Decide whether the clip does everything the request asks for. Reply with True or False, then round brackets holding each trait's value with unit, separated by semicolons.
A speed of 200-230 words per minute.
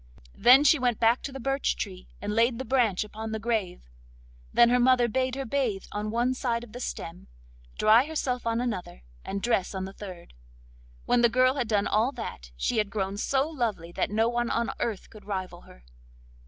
True (205 wpm)